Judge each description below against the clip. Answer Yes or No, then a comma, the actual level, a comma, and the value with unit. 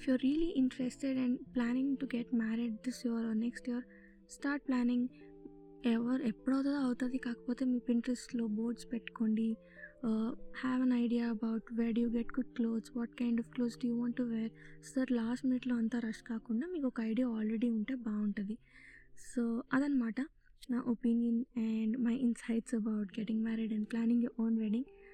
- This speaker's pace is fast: Yes, fast, 160 wpm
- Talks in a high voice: Yes, high, 235 Hz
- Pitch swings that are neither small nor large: No, narrow, 1.9 semitones